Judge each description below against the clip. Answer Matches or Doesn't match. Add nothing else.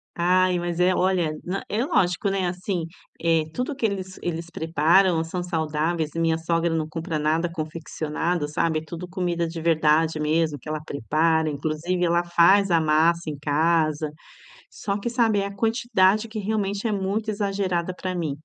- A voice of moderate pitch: Matches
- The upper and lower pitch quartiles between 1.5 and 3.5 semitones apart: Matches